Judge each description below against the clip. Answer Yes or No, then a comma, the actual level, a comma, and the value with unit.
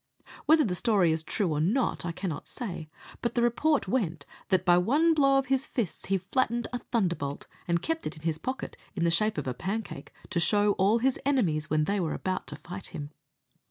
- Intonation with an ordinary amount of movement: No, wide, 6.4 semitones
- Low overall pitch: No, high, 195 Hz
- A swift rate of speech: Yes, fast, 220 wpm